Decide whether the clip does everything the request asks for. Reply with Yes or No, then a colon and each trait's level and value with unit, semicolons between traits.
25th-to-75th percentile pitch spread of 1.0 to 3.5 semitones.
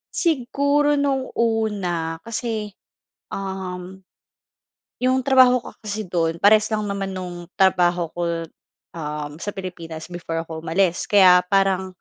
No: average, 4.2 semitones